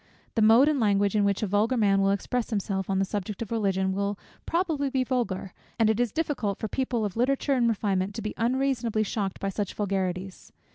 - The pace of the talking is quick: Yes, fast, 220 wpm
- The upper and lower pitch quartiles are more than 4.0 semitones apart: No, average, 3.7 semitones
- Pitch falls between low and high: No, high, 215 Hz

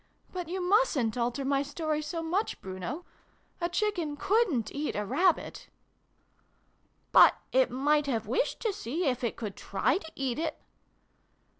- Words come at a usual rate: Yes, average, 160 wpm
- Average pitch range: No, wide, 6.2 semitones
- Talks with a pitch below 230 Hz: No, very high, 300 Hz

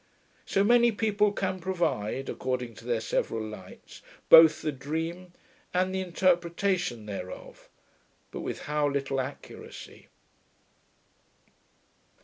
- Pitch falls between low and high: Yes, medium, 160 Hz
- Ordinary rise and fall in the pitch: No, wide, 6.5 semitones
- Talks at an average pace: No, slow, 110 wpm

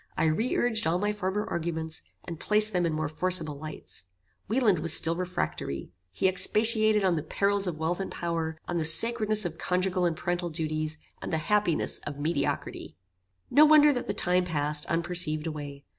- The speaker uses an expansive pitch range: No, average, 4.3 semitones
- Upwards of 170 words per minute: Yes, average, 180 wpm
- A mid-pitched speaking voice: Yes, medium, 175 Hz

